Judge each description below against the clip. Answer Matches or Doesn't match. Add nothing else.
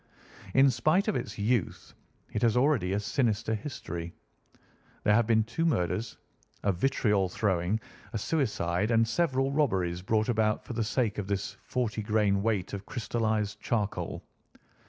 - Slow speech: Doesn't match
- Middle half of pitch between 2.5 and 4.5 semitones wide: Matches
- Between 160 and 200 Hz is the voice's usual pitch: Doesn't match